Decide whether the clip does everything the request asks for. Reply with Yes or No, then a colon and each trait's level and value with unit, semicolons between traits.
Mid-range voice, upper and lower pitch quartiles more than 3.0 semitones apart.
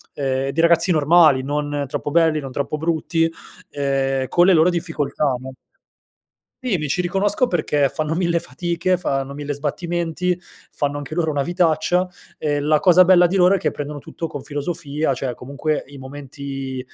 Yes: medium, 150 Hz; average, 3.6 semitones